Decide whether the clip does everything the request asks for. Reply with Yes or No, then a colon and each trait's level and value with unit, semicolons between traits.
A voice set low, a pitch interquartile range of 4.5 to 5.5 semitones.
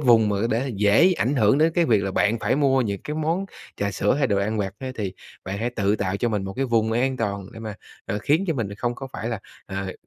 Yes: low, 110 Hz; average, 4.8 semitones